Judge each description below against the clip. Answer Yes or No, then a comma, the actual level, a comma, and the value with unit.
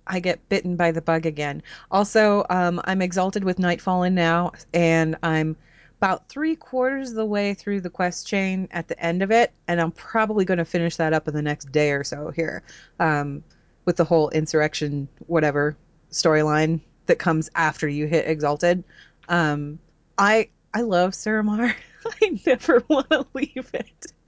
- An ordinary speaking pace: Yes, average, 175 wpm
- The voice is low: No, medium, 170 Hz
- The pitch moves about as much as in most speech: Yes, average, 3.9 semitones